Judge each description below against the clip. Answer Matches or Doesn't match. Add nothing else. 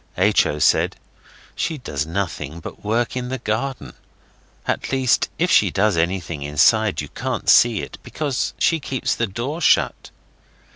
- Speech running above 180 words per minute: Doesn't match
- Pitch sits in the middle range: Doesn't match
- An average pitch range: Doesn't match